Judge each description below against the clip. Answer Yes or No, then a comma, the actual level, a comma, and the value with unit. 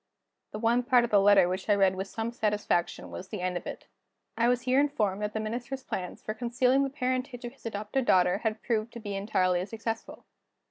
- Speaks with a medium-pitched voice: No, high, 220 Hz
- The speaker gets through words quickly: Yes, fast, 220 wpm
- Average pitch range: Yes, average, 3.6 semitones